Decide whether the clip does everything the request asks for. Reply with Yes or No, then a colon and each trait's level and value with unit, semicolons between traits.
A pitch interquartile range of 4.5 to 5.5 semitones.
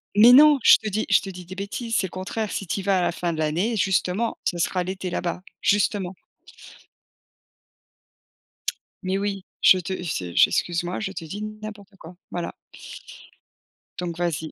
No: average, 2.9 semitones